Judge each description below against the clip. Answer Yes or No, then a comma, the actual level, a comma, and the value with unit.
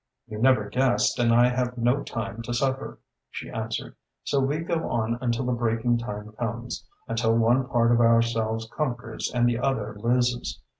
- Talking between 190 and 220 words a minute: No, average, 170 wpm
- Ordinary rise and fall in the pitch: No, narrow, 1.5 semitones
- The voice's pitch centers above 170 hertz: No, low, 120 Hz